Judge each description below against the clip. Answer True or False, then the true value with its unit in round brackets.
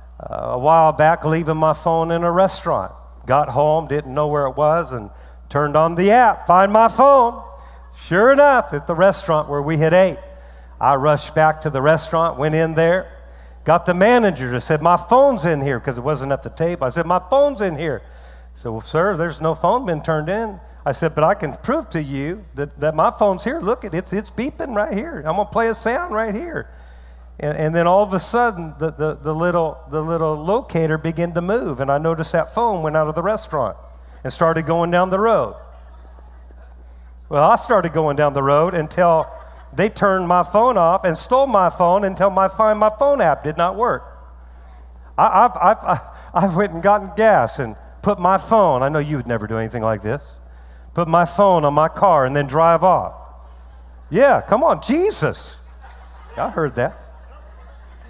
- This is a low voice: False (160 Hz)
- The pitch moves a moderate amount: False (7.1 semitones)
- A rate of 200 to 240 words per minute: True (205 wpm)